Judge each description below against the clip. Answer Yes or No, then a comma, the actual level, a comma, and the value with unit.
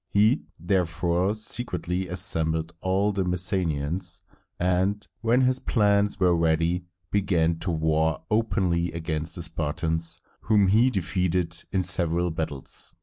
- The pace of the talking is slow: Yes, slow, 120 wpm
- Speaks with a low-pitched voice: Yes, very low, 90 Hz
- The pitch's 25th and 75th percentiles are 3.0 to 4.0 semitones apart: Yes, average, 3.3 semitones